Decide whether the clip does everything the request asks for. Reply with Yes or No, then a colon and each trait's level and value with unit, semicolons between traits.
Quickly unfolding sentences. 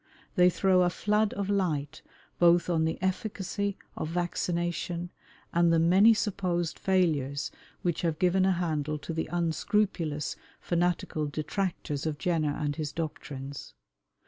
No: slow, 135 wpm